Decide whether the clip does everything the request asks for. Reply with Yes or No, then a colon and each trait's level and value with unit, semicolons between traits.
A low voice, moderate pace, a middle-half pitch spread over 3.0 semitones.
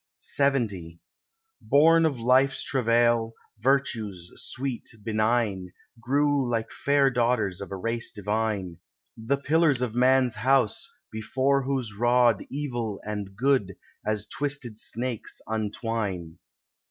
No: low, 120 Hz; slow, 110 wpm; average, 4.1 semitones